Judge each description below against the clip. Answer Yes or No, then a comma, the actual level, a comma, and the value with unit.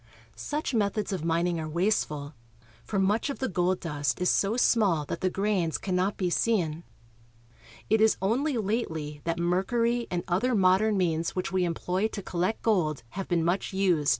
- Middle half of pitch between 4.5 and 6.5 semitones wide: No, average, 4.1 semitones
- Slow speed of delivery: No, average, 180 wpm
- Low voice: No, medium, 185 Hz